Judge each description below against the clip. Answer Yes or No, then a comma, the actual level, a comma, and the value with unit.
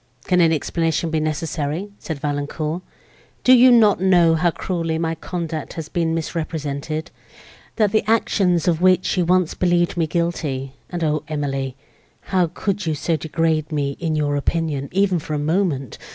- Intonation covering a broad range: No, average, 2.8 semitones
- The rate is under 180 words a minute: Yes, average, 165 wpm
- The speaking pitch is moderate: Yes, medium, 165 Hz